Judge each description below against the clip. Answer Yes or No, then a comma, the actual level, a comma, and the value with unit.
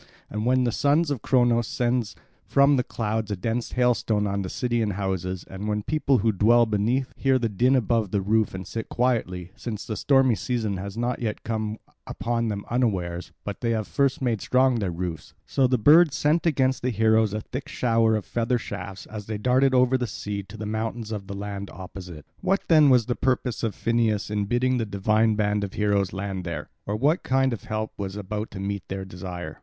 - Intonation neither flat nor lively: Yes, average, 3.7 semitones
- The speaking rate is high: Yes, fast, 210 wpm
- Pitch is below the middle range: Yes, low, 110 Hz